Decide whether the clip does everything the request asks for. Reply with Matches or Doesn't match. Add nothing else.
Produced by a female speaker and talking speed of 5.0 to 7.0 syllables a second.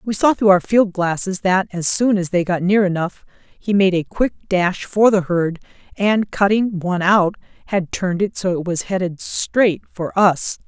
Doesn't match